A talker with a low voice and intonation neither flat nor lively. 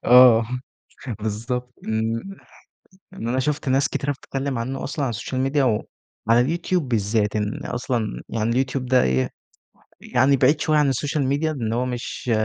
Yes: low, 125 Hz; average, 3.3 semitones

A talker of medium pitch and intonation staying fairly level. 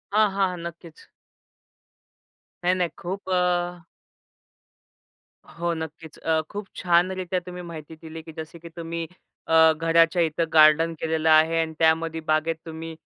Yes: medium, 165 Hz; narrow, 1.4 semitones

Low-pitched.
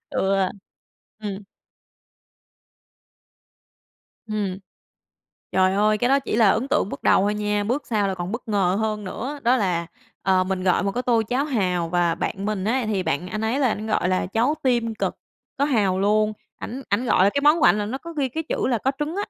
No: high, 215 Hz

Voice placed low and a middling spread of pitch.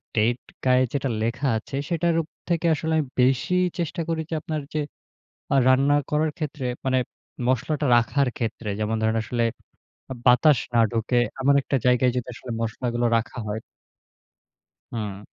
Yes: low, 130 Hz; average, 4.3 semitones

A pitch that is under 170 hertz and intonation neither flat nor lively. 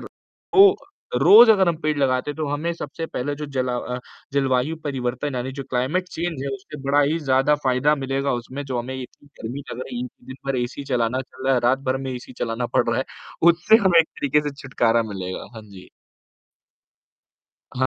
Yes: low, 135 Hz; average, 3.0 semitones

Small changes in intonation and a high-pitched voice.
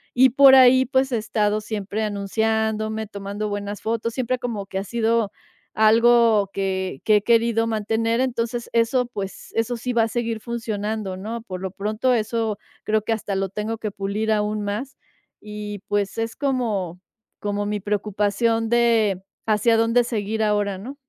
Yes: narrow, 2.1 semitones; high, 220 Hz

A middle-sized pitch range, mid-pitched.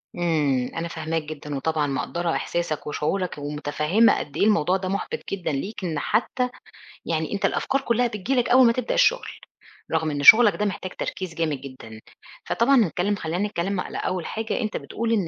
No: wide, 5.7 semitones; medium, 175 Hz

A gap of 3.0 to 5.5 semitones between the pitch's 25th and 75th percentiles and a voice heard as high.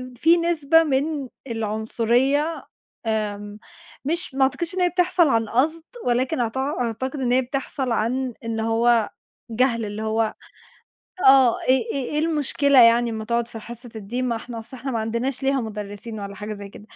Yes: average, 3.6 semitones; high, 245 Hz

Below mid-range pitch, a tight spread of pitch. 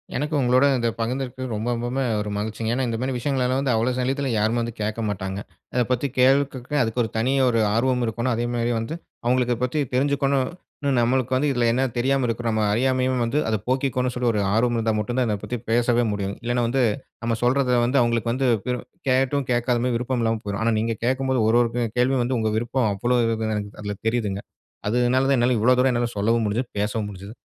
Yes: low, 120 Hz; narrow, 2.3 semitones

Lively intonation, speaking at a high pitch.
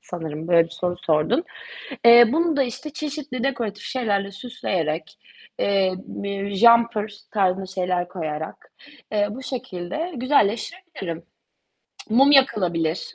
Yes: wide, 6.2 semitones; high, 200 Hz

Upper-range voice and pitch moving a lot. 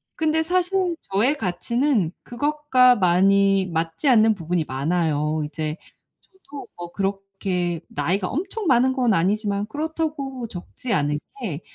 Yes: high, 200 Hz; wide, 8.1 semitones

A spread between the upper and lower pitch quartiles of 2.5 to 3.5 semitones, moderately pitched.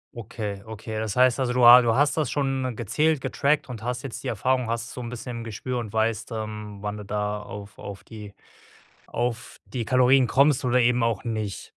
No: average, 2.9 semitones; low, 115 Hz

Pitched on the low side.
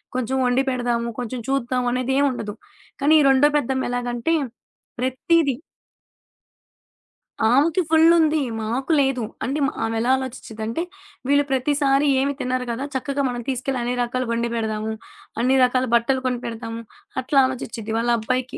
No: very high, 255 Hz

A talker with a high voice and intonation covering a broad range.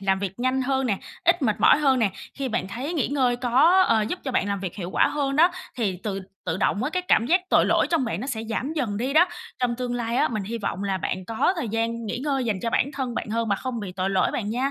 No: high, 235 Hz; average, 4.9 semitones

